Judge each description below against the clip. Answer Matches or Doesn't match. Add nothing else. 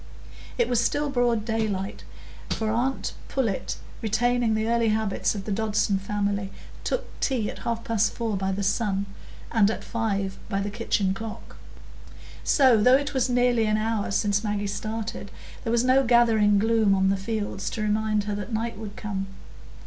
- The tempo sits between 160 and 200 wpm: Matches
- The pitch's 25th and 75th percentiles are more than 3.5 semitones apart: Doesn't match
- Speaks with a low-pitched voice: Doesn't match